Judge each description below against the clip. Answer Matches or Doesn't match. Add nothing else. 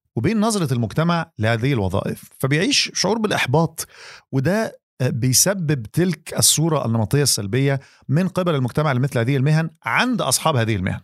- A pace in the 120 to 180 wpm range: Matches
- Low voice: Doesn't match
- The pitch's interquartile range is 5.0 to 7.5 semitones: Matches